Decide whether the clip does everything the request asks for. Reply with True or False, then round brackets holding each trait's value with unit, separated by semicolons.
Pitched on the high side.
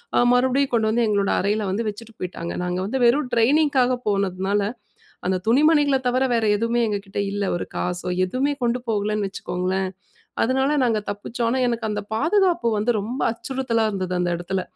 True (225 Hz)